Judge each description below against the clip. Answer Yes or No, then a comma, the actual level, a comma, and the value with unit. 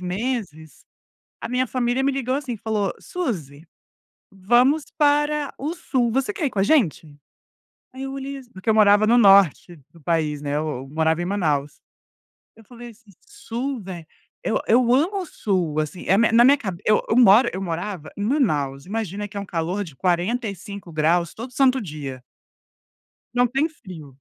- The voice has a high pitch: Yes, high, 205 Hz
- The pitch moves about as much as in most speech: No, wide, 7.0 semitones